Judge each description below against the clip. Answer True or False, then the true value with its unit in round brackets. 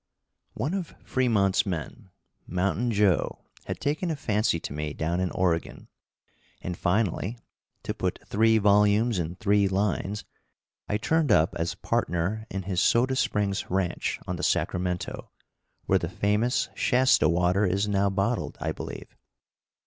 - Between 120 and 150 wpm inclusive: True (140 wpm)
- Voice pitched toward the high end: False (100 Hz)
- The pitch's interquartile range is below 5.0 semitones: True (3.7 semitones)